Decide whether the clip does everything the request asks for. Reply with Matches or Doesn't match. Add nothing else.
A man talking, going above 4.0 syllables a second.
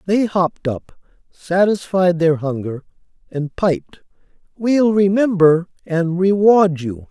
Doesn't match